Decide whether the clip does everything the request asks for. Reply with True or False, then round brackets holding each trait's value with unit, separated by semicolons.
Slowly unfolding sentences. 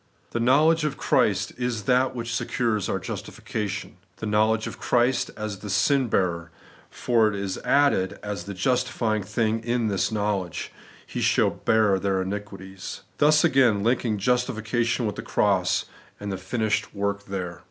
False (160 wpm)